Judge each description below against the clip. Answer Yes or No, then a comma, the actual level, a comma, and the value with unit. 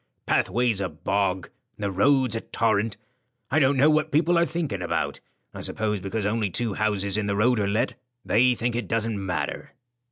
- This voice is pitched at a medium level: No, low, 110 Hz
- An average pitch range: Yes, average, 4.0 semitones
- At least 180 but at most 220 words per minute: Yes, average, 190 wpm